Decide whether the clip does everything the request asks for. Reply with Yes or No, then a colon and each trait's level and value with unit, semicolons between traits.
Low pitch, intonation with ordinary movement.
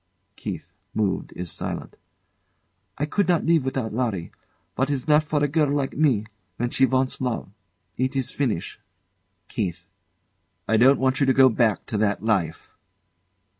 Yes: low, 130 Hz; average, 4.6 semitones